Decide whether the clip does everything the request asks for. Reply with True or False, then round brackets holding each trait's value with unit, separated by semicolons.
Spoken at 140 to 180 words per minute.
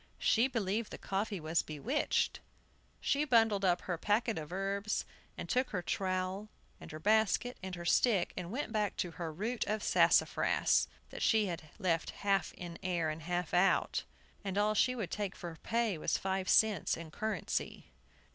True (175 wpm)